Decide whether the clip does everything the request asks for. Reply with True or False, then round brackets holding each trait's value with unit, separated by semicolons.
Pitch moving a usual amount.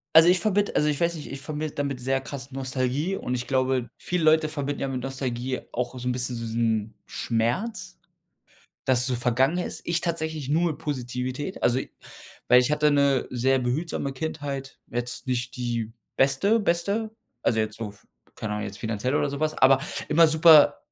True (3.9 semitones)